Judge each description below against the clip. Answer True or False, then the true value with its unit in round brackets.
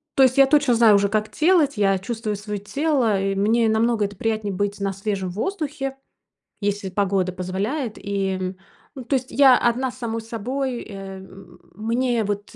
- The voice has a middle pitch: False (215 Hz)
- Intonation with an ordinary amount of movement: True (4.3 semitones)